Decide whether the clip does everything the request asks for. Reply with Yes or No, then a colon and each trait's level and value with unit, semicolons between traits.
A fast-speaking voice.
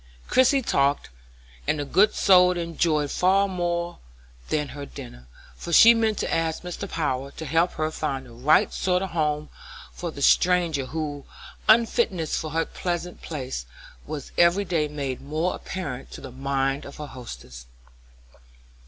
No: average, 160 wpm